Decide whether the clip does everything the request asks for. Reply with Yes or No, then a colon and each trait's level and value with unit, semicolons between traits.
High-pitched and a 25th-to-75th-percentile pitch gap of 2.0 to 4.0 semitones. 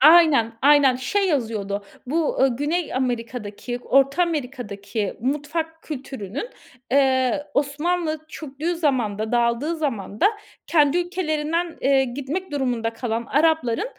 No: very high, 275 Hz; average, 4.7 semitones